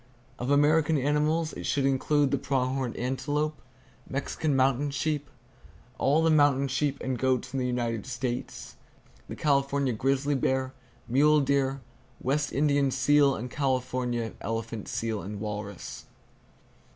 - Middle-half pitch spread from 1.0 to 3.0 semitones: Yes, narrow, 2.4 semitones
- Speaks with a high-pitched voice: No, low, 135 Hz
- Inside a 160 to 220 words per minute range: No, slow, 135 wpm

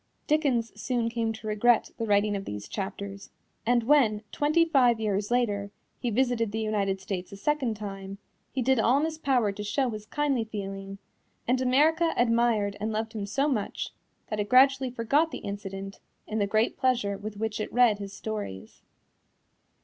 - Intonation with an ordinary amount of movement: Yes, average, 3.9 semitones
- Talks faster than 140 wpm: Yes, average, 180 wpm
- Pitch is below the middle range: No, high, 220 Hz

